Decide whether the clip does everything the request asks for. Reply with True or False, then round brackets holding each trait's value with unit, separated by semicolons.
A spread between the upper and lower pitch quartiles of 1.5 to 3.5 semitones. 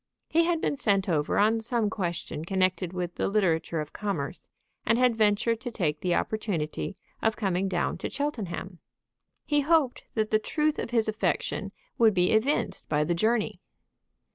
False (4.7 semitones)